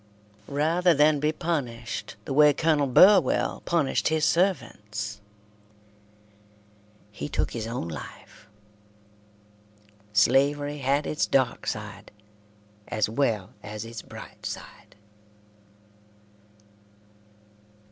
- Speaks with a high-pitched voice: No, low, 135 Hz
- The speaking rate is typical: No, slow, 90 wpm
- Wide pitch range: Yes, wide, 5.9 semitones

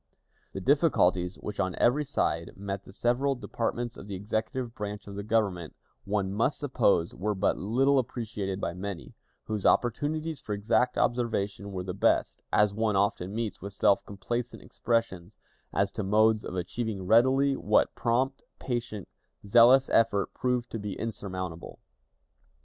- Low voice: Yes, low, 105 Hz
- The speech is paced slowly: No, average, 150 wpm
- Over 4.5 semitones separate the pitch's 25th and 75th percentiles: No, average, 3.7 semitones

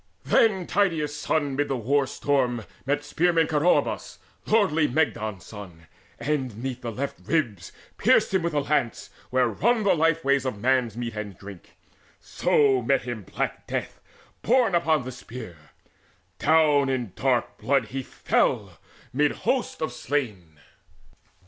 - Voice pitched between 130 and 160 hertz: Yes, low, 135 Hz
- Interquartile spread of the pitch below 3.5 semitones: No, average, 4.9 semitones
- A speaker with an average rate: Yes, average, 145 wpm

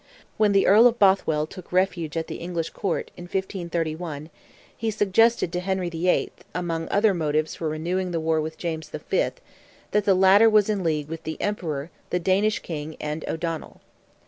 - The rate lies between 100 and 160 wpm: No, average, 175 wpm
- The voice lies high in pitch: No, medium, 175 Hz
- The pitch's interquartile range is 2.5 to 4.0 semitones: Yes, average, 3.4 semitones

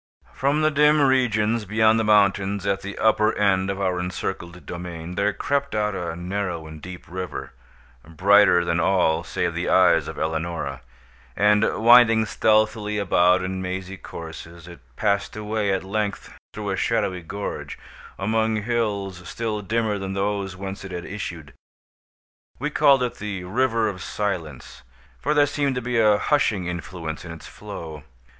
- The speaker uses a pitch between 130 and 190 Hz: No, low, 100 Hz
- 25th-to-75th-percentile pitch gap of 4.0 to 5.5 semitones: No, average, 3.5 semitones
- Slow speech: No, average, 160 wpm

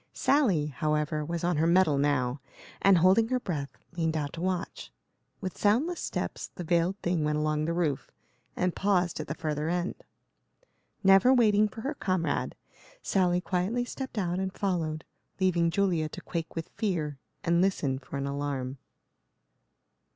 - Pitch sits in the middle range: Yes, medium, 170 Hz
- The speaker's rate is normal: Yes, average, 160 wpm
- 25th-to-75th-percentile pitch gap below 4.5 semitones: Yes, average, 4.0 semitones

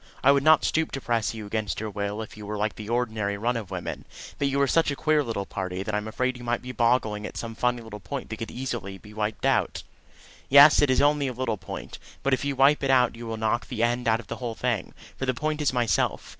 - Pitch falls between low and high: No, low, 120 Hz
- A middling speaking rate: No, fast, 265 wpm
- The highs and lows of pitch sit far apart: No, average, 3.7 semitones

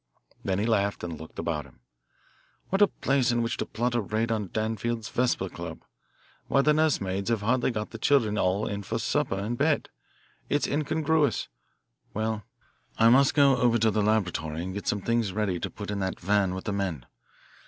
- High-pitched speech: No, low, 110 Hz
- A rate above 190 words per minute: Yes, average, 200 wpm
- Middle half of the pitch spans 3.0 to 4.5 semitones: Yes, average, 3.8 semitones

